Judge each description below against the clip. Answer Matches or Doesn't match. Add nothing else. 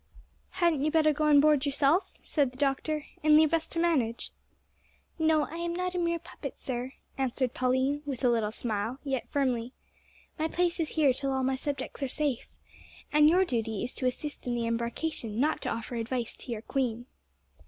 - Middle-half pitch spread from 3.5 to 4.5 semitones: Matches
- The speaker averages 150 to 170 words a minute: Doesn't match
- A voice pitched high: Matches